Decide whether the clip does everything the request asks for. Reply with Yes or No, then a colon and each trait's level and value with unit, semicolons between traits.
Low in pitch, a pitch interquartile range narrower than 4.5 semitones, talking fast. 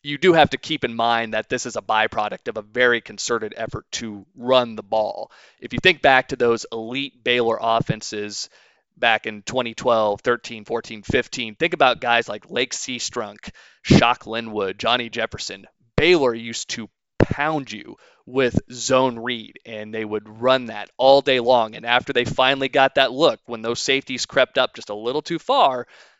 No: low, 120 Hz; average, 2.8 semitones; average, 180 wpm